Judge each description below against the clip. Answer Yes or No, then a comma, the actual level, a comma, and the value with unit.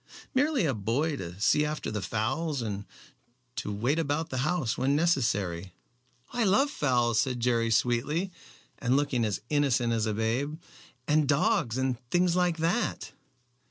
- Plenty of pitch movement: Yes, wide, 5.9 semitones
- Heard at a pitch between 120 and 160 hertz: Yes, low, 135 Hz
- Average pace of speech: Yes, average, 155 wpm